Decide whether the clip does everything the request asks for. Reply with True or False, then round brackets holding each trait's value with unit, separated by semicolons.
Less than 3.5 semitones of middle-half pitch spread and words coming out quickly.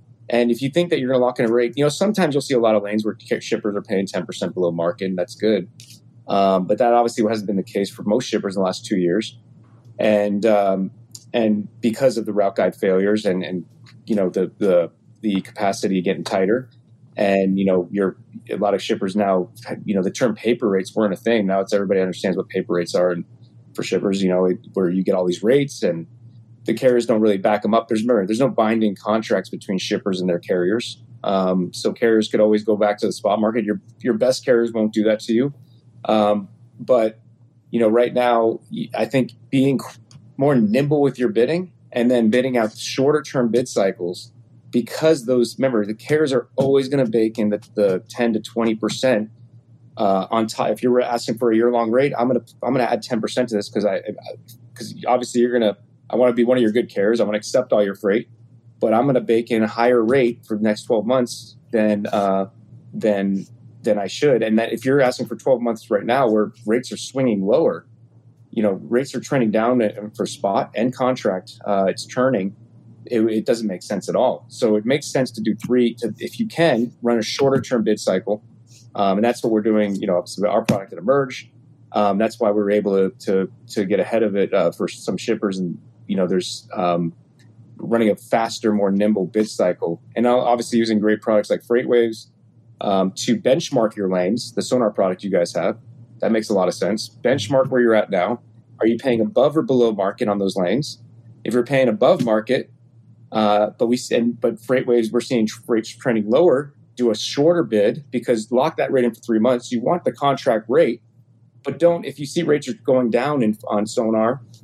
True (2.6 semitones; 220 wpm)